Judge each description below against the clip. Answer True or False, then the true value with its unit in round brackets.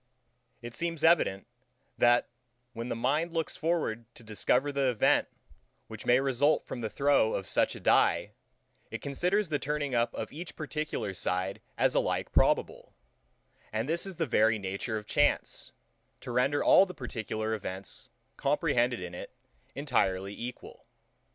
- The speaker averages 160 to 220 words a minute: False (150 wpm)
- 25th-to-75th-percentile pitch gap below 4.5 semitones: False (5.4 semitones)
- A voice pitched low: True (125 Hz)